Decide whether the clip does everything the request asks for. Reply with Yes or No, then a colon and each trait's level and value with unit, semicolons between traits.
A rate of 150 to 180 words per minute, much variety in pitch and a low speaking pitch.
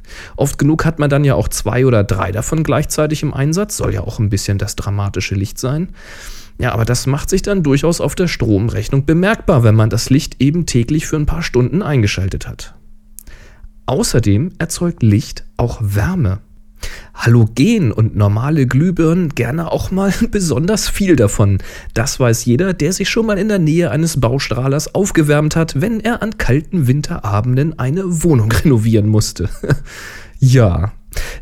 Yes: average, 160 wpm; wide, 7.2 semitones; low, 130 Hz